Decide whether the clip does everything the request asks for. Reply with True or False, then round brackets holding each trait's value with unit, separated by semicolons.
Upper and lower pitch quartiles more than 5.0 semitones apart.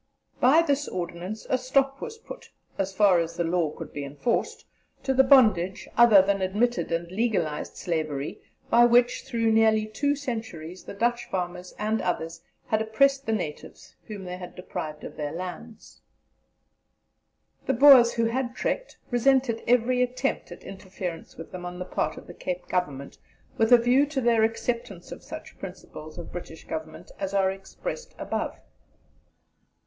True (5.5 semitones)